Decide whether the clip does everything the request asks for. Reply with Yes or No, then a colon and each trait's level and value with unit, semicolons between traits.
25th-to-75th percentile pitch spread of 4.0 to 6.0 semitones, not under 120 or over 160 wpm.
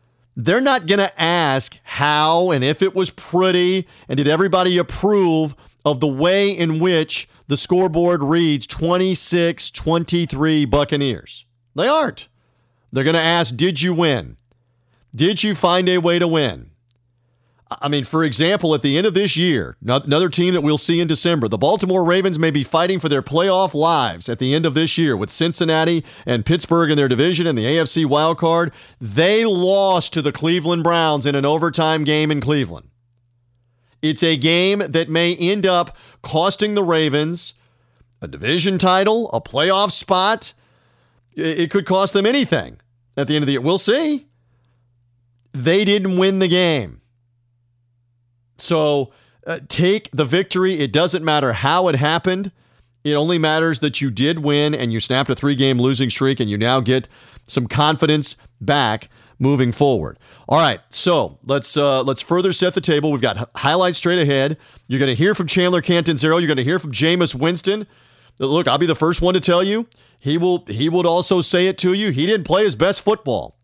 No: average, 4.9 semitones; average, 180 wpm